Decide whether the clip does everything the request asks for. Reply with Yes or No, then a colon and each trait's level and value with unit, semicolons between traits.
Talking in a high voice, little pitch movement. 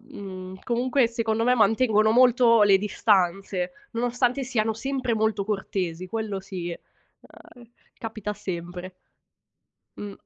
No: high, 215 Hz; average, 3.7 semitones